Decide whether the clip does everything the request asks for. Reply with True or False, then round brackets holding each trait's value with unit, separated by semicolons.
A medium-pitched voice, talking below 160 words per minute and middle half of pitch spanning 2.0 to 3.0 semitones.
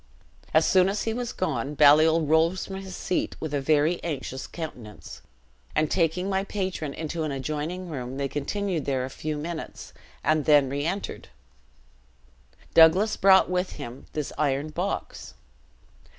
False (155 Hz; 150 wpm; 4.1 semitones)